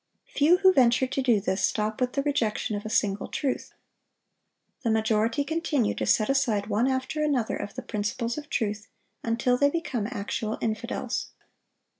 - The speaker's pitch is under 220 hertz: No, high, 235 Hz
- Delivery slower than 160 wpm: No, average, 165 wpm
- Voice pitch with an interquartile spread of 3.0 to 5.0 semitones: Yes, average, 4.4 semitones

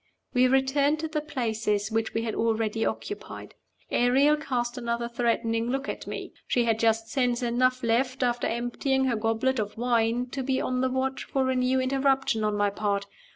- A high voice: Yes, high, 245 Hz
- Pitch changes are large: No, narrow, 2.6 semitones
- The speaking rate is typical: Yes, average, 185 wpm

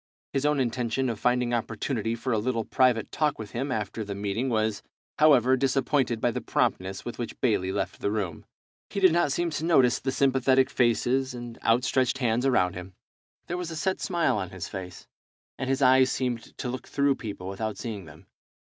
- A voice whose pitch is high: No, low, 125 Hz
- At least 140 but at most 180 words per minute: No, average, 200 wpm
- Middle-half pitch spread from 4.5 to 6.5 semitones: No, average, 3.6 semitones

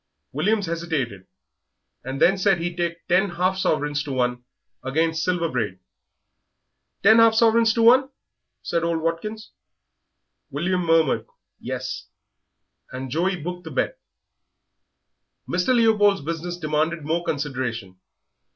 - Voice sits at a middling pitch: Yes, medium, 170 Hz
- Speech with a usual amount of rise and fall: Yes, average, 4.6 semitones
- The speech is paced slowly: Yes, slow, 120 wpm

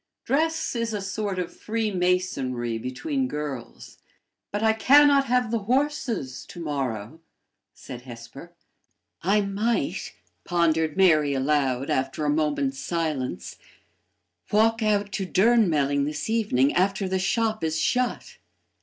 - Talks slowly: Yes, slow, 125 wpm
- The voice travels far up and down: Yes, wide, 7.7 semitones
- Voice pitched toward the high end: No, medium, 180 Hz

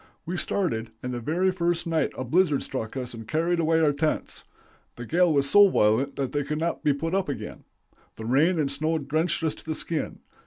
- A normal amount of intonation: Yes, average, 3.7 semitones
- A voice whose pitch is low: No, medium, 155 Hz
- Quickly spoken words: Yes, fast, 220 wpm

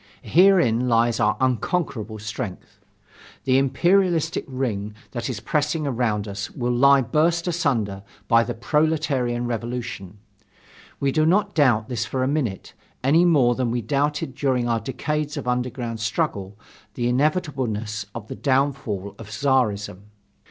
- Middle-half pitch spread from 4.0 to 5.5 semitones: Yes, average, 4.3 semitones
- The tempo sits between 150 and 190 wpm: No, average, 140 wpm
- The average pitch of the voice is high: No, low, 125 Hz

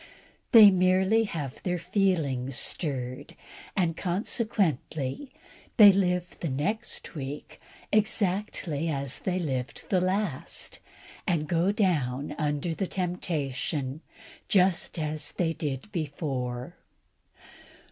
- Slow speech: Yes, slow, 100 wpm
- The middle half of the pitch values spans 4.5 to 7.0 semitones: Yes, average, 5.1 semitones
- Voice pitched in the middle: Yes, medium, 165 Hz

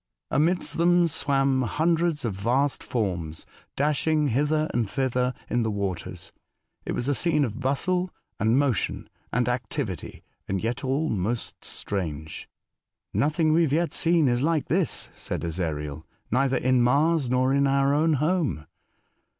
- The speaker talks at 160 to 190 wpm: No, average, 145 wpm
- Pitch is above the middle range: No, low, 135 Hz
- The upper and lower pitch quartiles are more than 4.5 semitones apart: Yes, wide, 5.4 semitones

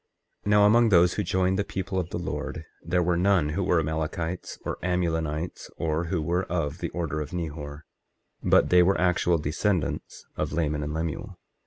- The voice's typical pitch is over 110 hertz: No, very low, 85 Hz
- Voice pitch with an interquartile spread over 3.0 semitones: No, average, 2.7 semitones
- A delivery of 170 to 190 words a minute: Yes, average, 185 wpm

